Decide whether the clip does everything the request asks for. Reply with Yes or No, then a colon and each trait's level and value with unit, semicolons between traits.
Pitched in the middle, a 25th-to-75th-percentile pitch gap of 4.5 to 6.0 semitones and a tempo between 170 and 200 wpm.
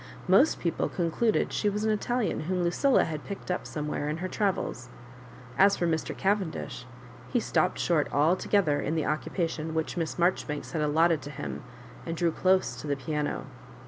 No: medium, 170 Hz; average, 3.8 semitones; average, 180 wpm